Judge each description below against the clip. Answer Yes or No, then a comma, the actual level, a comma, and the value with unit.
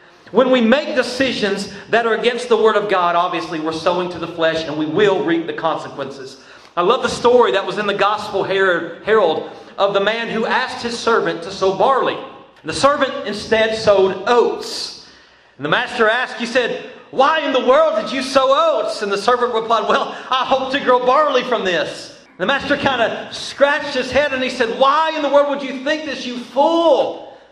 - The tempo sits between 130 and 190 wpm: No, fast, 205 wpm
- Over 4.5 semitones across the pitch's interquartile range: Yes, wide, 5.4 semitones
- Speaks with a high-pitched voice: Yes, high, 235 Hz